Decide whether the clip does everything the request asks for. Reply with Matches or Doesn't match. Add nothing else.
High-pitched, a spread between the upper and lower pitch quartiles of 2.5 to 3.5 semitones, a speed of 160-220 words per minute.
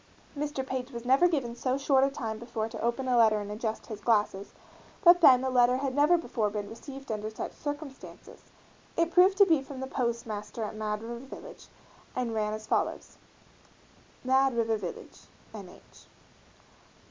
Doesn't match